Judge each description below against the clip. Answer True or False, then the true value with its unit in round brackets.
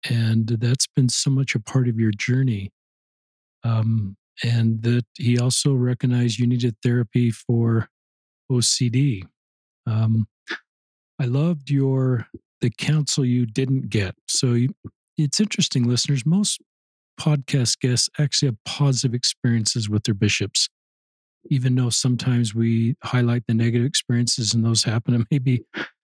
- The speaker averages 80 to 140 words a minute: True (135 wpm)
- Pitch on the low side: True (120 Hz)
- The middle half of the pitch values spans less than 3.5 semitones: True (2.7 semitones)